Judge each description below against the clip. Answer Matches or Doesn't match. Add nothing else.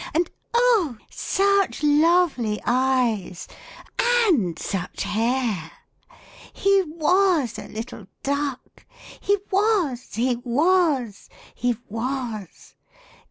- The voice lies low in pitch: Doesn't match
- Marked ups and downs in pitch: Matches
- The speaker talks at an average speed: Doesn't match